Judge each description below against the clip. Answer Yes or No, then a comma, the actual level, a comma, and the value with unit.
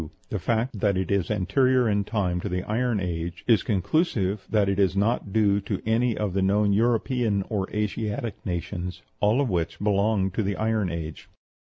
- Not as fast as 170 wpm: No, average, 185 wpm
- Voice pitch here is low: Yes, low, 100 Hz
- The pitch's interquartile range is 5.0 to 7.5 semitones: No, average, 2.9 semitones